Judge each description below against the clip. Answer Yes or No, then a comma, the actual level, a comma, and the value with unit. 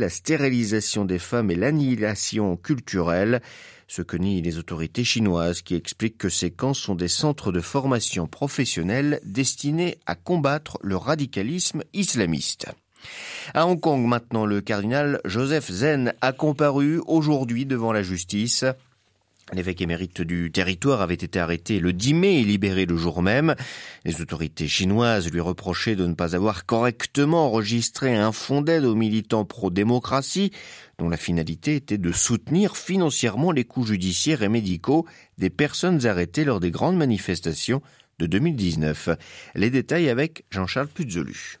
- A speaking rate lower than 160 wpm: Yes, slow, 145 wpm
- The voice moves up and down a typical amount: No, wide, 7.4 semitones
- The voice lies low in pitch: Yes, low, 115 Hz